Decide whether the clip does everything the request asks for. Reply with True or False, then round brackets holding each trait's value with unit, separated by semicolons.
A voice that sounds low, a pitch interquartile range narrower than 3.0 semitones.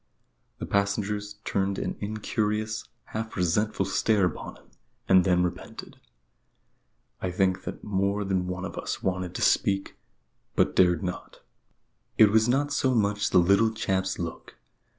True (100 Hz; 2.4 semitones)